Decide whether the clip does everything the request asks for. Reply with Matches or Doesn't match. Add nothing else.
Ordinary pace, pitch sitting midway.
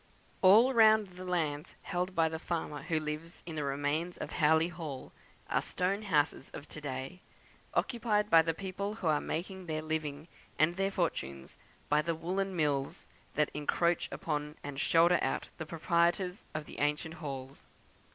Matches